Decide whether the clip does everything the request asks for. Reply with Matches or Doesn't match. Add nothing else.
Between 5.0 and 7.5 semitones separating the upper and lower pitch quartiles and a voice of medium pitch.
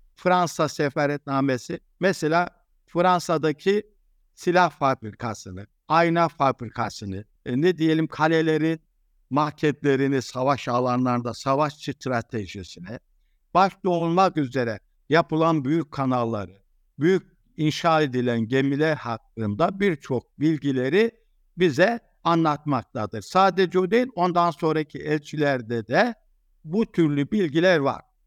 Matches